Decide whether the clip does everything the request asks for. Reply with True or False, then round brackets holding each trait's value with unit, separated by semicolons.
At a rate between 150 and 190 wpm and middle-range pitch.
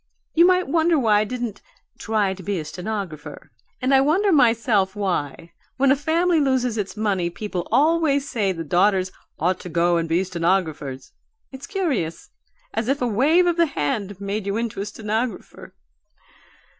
False (170 wpm; 210 Hz)